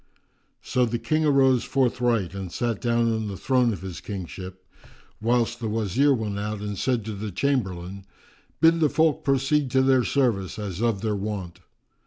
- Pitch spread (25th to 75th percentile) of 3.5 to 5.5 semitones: Yes, average, 4.8 semitones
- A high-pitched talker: No, low, 115 Hz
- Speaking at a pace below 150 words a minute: No, average, 175 wpm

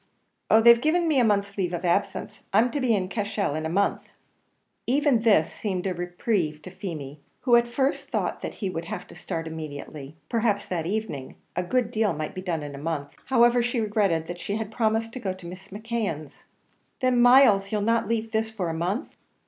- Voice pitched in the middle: No, high, 200 Hz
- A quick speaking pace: Yes, fast, 215 wpm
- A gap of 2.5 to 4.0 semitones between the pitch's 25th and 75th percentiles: No, average, 5.3 semitones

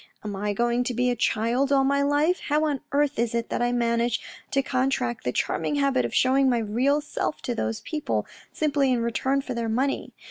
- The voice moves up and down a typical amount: Yes, average, 3.1 semitones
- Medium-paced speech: No, fast, 220 wpm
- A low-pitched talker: No, very high, 255 Hz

